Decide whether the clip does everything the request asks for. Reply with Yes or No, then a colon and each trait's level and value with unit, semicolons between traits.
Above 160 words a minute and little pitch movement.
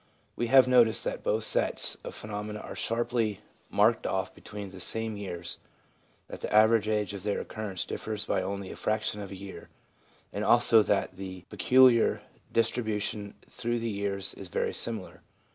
Yes: average, 170 wpm; narrow, 2.3 semitones